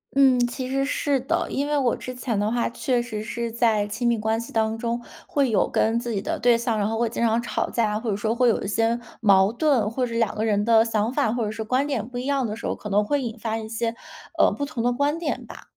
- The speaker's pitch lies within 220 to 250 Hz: Yes, high, 235 Hz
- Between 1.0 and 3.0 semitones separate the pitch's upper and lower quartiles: Yes, narrow, 2.5 semitones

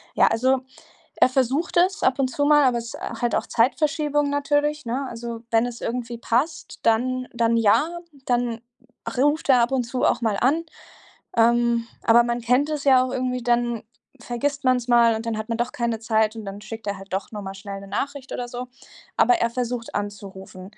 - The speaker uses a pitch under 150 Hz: No, high, 240 Hz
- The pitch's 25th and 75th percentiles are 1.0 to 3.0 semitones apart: Yes, narrow, 2.6 semitones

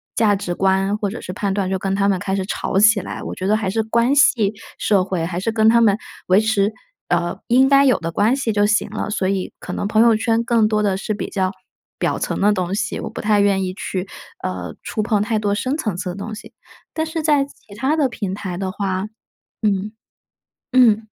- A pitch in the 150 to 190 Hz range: No, high, 205 Hz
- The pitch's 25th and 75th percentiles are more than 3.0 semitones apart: No, average, 2.7 semitones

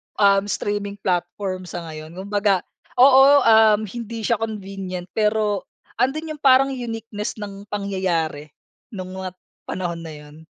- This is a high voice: Yes, high, 205 Hz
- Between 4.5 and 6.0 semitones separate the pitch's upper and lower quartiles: No, average, 3.5 semitones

